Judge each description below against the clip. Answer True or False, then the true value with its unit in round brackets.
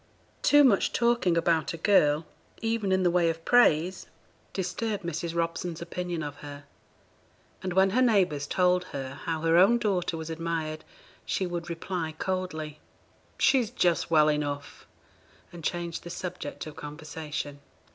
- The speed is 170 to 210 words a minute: False (145 wpm)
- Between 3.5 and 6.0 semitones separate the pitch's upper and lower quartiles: False (3.1 semitones)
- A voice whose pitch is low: False (170 Hz)